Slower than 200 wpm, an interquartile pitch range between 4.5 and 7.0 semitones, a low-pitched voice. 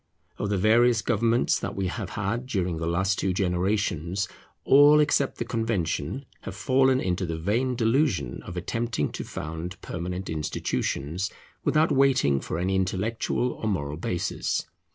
Yes: average, 150 wpm; average, 5.2 semitones; very low, 95 Hz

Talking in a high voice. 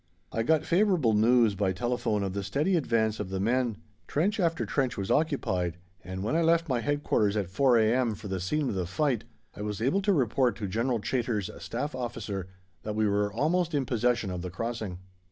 No: low, 115 Hz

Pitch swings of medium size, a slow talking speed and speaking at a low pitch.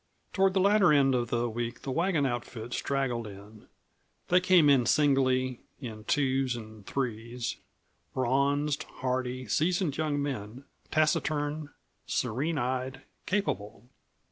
Yes: average, 3.8 semitones; slow, 120 wpm; low, 130 Hz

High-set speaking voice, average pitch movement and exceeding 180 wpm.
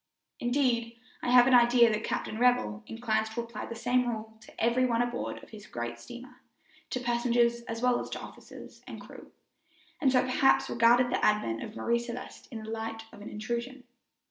No: high, 235 Hz; narrow, 1.8 semitones; average, 195 wpm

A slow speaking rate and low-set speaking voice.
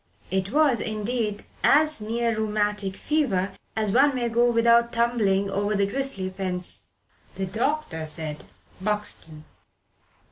No: slow, 120 wpm; high, 215 Hz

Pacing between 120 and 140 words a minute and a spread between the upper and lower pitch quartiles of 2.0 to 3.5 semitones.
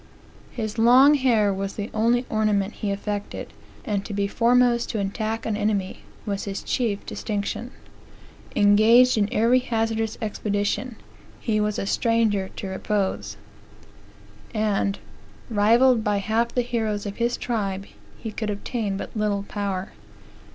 Yes: slow, 135 wpm; narrow, 2.4 semitones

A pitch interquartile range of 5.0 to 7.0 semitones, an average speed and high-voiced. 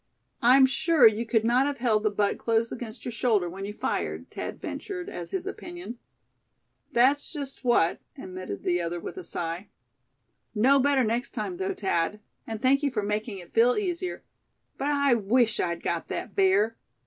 Yes: average, 5.3 semitones; average, 180 wpm; high, 235 Hz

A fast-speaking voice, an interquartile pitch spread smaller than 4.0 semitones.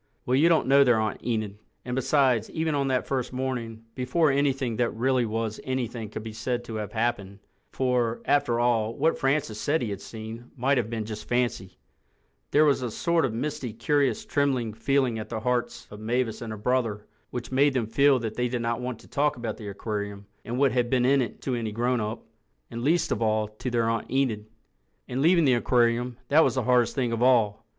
Yes: fast, 210 wpm; average, 3.0 semitones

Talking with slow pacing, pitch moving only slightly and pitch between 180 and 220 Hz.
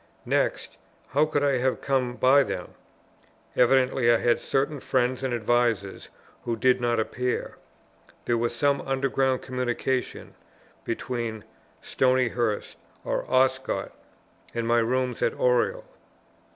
No: slow, 120 wpm; narrow, 2.0 semitones; low, 125 Hz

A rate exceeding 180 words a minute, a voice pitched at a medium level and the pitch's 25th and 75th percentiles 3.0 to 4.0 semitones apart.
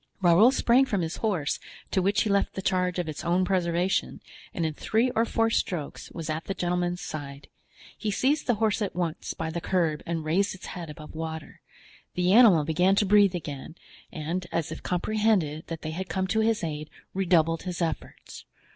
Yes: average, 200 wpm; medium, 180 Hz; average, 3.7 semitones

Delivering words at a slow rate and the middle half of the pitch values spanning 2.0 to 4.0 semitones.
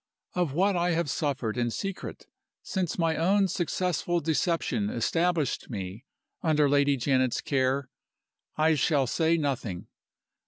No: slow, 125 wpm; average, 4.6 semitones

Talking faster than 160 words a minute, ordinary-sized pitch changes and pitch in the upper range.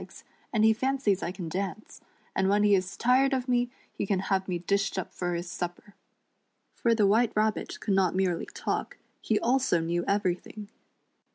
Yes: average, 185 wpm; average, 3.3 semitones; high, 200 Hz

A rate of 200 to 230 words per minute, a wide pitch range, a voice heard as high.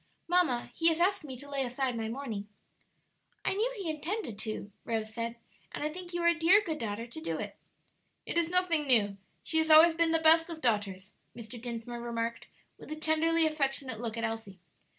Yes: fast, 205 wpm; wide, 6.2 semitones; very high, 280 Hz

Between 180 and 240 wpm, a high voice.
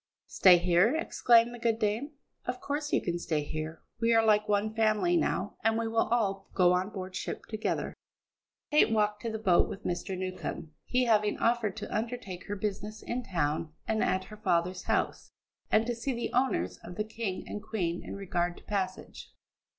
Yes: average, 190 wpm; high, 210 Hz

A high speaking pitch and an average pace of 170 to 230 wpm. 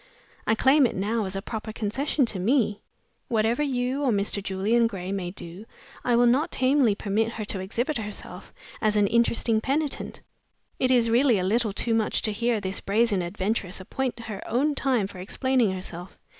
Yes: high, 225 Hz; average, 185 wpm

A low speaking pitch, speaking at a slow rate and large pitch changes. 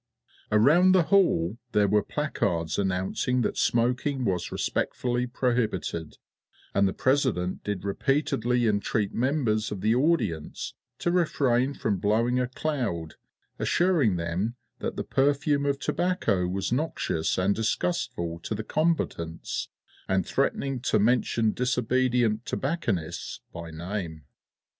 Yes: low, 115 Hz; slow, 120 wpm; wide, 6.1 semitones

